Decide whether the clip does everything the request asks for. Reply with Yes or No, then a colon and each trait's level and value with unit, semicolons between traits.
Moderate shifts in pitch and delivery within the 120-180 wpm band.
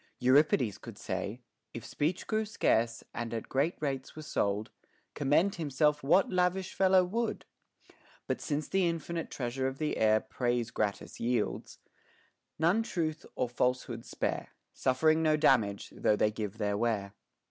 No: wide, 6.1 semitones; average, 145 wpm